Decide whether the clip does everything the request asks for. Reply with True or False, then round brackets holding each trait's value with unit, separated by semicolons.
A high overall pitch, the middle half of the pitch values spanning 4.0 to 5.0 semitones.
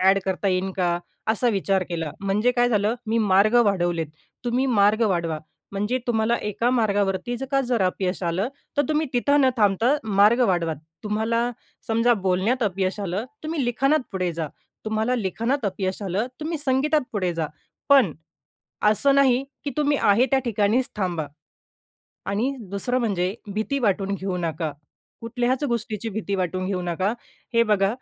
True (210 Hz; 4.4 semitones)